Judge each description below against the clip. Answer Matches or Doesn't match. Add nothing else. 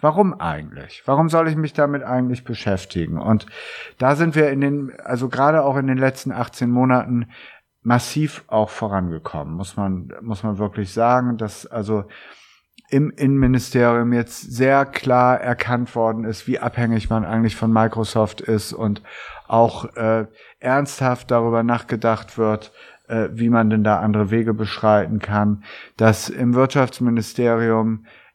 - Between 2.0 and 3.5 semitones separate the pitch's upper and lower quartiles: Matches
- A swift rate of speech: Doesn't match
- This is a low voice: Matches